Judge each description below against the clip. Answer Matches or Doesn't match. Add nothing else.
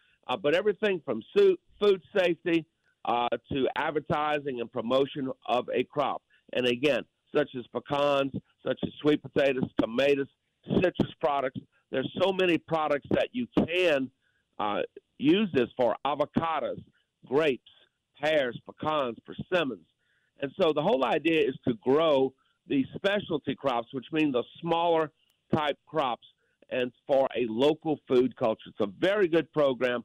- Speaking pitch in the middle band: Matches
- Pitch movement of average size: Matches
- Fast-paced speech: Doesn't match